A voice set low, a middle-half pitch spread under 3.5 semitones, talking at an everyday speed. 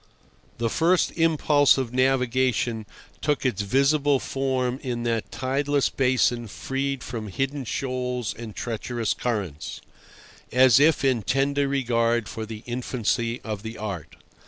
No: low, 125 Hz; average, 2.9 semitones; slow, 130 wpm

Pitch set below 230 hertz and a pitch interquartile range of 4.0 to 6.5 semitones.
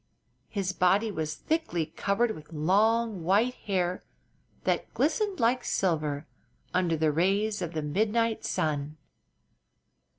Yes: medium, 185 Hz; wide, 5.6 semitones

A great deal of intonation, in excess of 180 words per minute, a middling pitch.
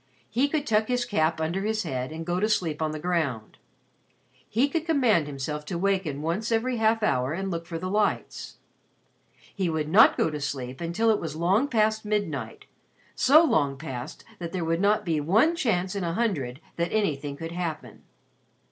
Yes: wide, 6.0 semitones; average, 190 wpm; medium, 175 Hz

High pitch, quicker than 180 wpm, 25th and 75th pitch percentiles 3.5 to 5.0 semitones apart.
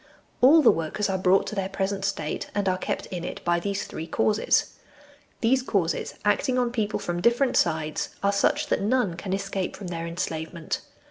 Yes: high, 195 Hz; average, 190 wpm; average, 3.8 semitones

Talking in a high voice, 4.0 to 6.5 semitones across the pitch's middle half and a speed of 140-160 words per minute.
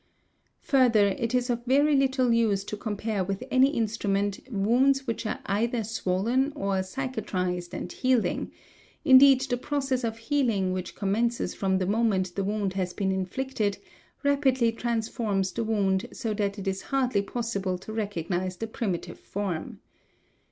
Yes: high, 220 Hz; average, 4.4 semitones; average, 150 wpm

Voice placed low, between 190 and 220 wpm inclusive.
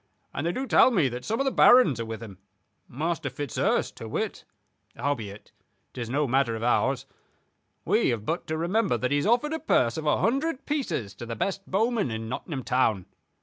No: medium, 145 Hz; average, 200 wpm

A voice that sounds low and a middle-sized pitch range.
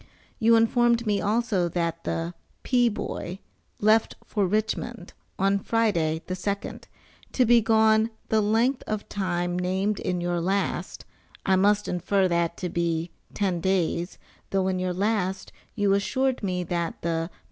No: high, 195 Hz; average, 3.7 semitones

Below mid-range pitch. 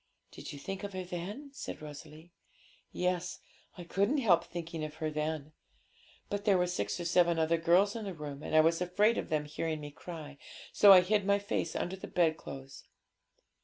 No: medium, 170 Hz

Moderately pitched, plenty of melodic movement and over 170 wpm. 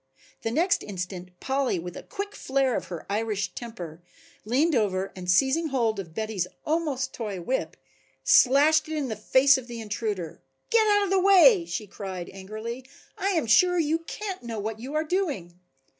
No: high, 240 Hz; wide, 7.9 semitones; average, 180 wpm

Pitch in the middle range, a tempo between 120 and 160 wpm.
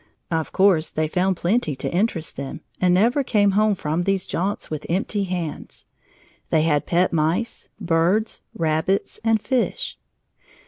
Yes: medium, 180 Hz; average, 145 wpm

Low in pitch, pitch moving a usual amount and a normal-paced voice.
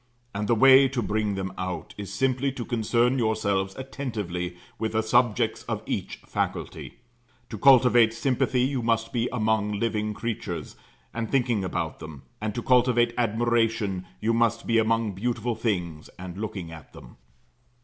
Yes: low, 115 Hz; average, 3.1 semitones; average, 155 wpm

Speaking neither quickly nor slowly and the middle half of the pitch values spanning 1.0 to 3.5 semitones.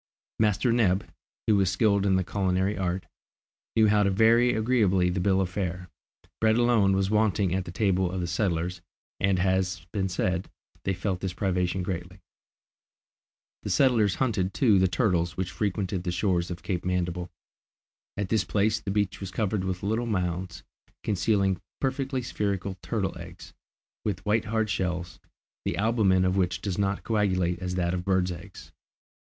Yes: average, 170 wpm; narrow, 2.6 semitones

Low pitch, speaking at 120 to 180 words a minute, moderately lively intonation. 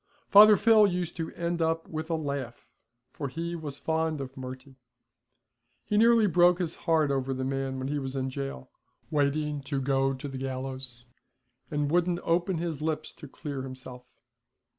No: medium, 145 Hz; average, 175 wpm; average, 3.9 semitones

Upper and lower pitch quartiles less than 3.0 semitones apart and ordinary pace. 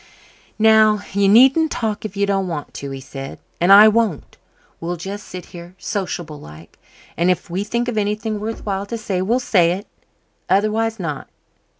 No: average, 3.8 semitones; average, 180 wpm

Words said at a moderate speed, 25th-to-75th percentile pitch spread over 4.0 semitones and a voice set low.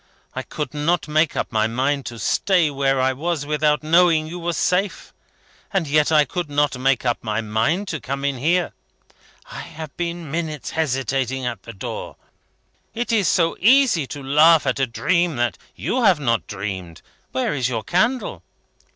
No: average, 175 wpm; average, 4.7 semitones; medium, 150 Hz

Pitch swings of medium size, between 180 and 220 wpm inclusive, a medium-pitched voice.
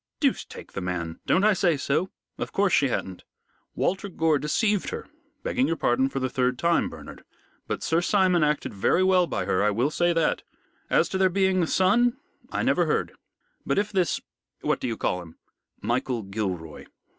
No: wide, 7.8 semitones; average, 190 wpm; medium, 165 Hz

